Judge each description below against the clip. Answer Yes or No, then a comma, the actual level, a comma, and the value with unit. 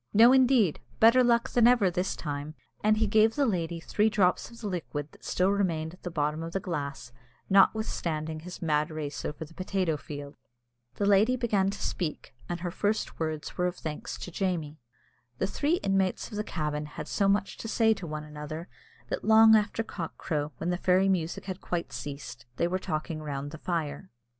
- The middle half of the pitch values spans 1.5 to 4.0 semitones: No, average, 5.0 semitones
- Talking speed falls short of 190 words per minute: No, average, 200 wpm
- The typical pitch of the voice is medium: Yes, medium, 180 Hz